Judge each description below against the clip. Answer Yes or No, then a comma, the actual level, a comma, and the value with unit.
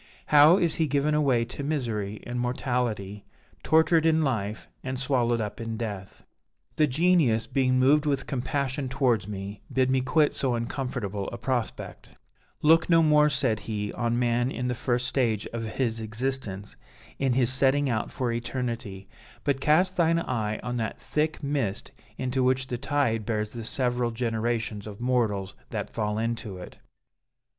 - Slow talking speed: No, average, 160 wpm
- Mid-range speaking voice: No, low, 125 Hz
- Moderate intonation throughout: Yes, average, 3.7 semitones